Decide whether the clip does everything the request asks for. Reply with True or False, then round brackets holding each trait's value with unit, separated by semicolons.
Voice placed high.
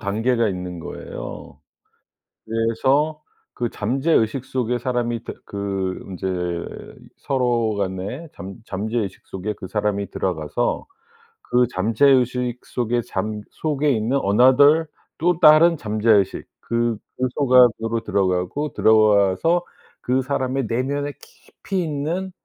False (120 Hz)